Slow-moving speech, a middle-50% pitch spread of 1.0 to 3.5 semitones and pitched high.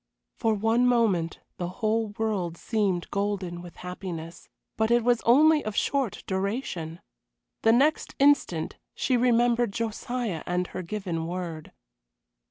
No: slow, 130 wpm; average, 5.1 semitones; high, 210 Hz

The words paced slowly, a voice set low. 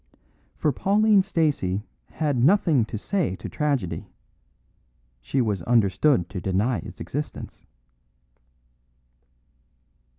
Yes: slow, 95 wpm; low, 130 Hz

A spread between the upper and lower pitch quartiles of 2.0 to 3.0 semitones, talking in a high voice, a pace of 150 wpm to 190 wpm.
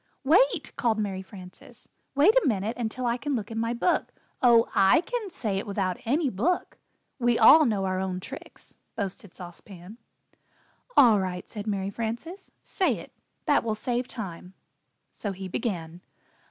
No: average, 4.8 semitones; high, 220 Hz; average, 165 wpm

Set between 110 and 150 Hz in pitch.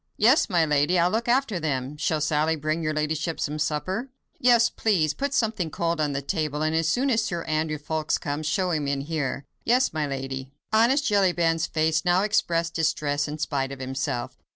No: medium, 160 Hz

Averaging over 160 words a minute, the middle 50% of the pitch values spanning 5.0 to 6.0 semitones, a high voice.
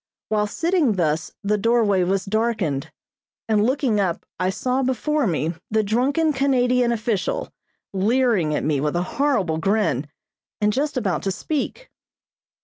No: average, 140 wpm; wide, 5.5 semitones; high, 215 Hz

